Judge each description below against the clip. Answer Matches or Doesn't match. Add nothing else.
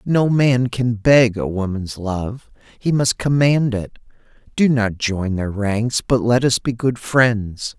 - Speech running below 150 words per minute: Doesn't match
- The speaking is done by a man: Matches